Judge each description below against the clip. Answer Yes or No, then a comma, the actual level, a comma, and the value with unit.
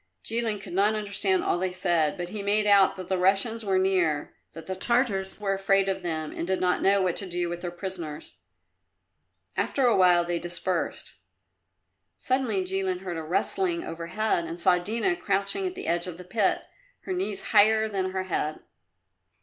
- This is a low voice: No, high, 190 Hz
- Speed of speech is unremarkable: Yes, average, 185 wpm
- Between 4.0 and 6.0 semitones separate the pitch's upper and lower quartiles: No, average, 3.0 semitones